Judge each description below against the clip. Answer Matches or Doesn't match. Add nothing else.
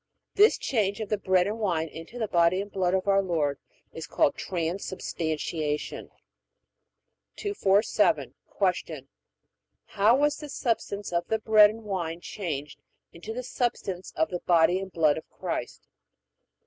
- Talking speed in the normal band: Matches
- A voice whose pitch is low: Doesn't match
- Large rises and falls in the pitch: Doesn't match